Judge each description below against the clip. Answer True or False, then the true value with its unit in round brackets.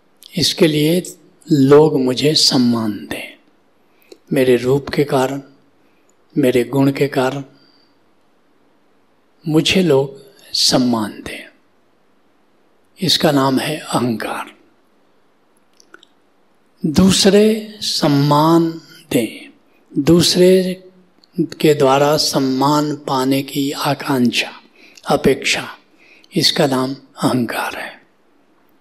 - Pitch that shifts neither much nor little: True (3.9 semitones)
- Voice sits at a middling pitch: True (150 Hz)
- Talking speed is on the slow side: True (75 wpm)